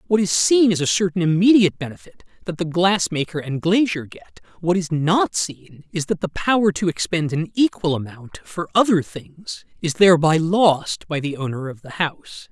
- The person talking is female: No, male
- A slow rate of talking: No, average, 190 wpm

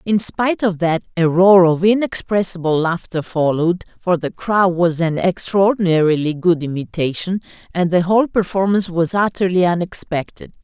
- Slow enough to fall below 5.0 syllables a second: No, 5.1 syllables/s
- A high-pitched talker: No, medium, 180 Hz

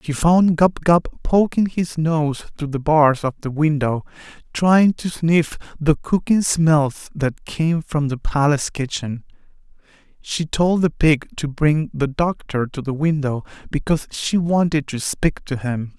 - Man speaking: Yes, male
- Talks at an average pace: Yes, average, 160 wpm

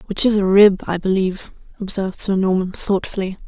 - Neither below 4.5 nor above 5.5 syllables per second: No, 5.8 syllables/s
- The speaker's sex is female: Yes, female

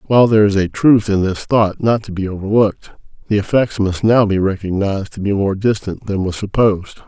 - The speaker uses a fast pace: Yes, fast, 210 wpm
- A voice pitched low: Yes, low, 100 Hz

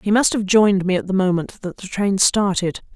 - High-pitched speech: Yes, high, 195 Hz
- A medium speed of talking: No, fast, 245 wpm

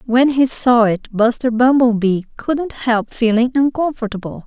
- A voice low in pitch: No, high, 240 Hz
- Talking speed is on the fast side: No, slow, 135 wpm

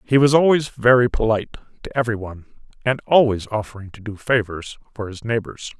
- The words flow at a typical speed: Yes, average, 175 wpm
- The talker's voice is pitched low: Yes, low, 115 Hz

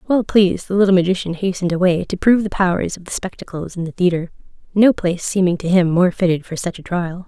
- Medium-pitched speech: Yes, medium, 180 Hz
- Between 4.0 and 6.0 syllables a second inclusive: No, 6.4 syllables/s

